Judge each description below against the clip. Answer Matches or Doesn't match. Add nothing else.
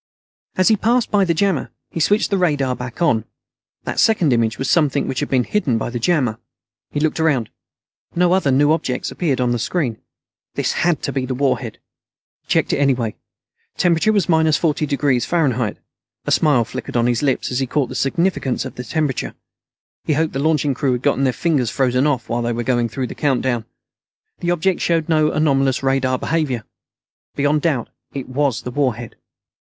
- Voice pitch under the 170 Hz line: Matches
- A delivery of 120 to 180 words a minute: Doesn't match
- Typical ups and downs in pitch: Matches